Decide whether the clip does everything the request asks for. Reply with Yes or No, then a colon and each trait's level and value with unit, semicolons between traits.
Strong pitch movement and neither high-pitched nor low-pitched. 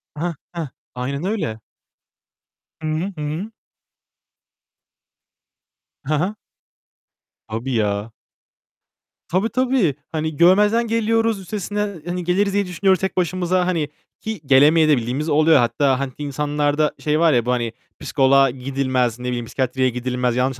Yes: wide, 6.0 semitones; medium, 150 Hz